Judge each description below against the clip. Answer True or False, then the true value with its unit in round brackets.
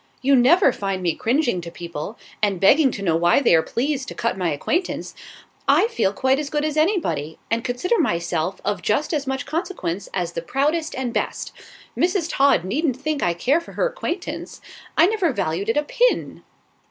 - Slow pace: False (190 wpm)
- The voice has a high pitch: True (260 Hz)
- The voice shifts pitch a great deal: True (8.9 semitones)